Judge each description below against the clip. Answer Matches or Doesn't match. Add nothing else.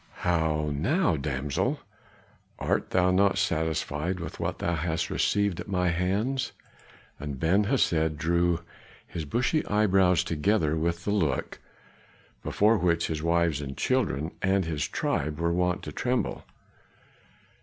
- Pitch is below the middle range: Matches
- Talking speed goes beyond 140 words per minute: Doesn't match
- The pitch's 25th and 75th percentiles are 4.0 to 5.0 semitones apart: Doesn't match